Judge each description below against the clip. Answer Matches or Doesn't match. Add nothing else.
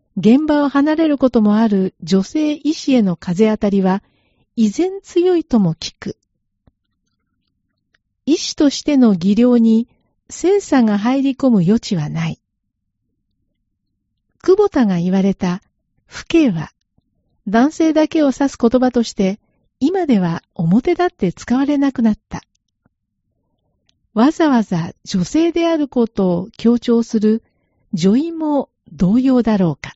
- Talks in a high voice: Matches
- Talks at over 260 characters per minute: Doesn't match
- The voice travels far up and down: Matches